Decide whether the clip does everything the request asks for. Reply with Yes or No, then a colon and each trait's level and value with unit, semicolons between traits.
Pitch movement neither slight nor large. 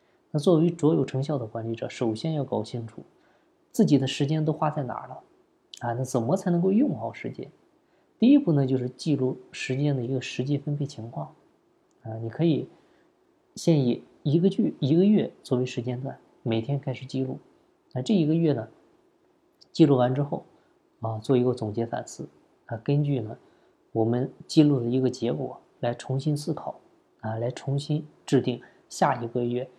Yes: average, 4.6 semitones